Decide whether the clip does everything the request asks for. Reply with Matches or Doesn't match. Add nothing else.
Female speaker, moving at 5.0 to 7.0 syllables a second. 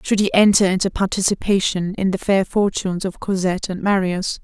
Matches